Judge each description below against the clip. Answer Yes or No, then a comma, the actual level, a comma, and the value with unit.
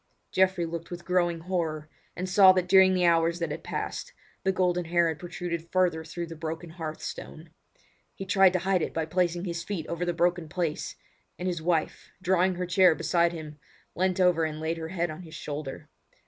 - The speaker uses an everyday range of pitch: No, narrow, 1.9 semitones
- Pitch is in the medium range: Yes, medium, 175 Hz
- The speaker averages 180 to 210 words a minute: Yes, fast, 205 wpm